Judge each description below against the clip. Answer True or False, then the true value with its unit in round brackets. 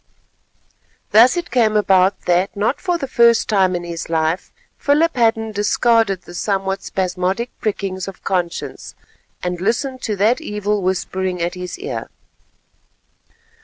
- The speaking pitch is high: True (200 Hz)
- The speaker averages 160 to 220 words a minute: False (135 wpm)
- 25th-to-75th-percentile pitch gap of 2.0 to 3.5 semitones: False (4.2 semitones)